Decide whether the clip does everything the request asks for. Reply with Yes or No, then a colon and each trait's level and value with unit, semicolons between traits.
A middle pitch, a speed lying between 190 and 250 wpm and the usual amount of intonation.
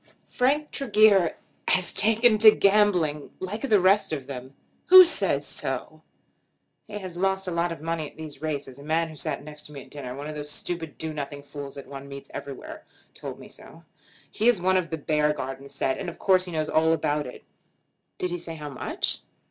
Yes: medium, 160 Hz; fast, 205 wpm; average, 5.0 semitones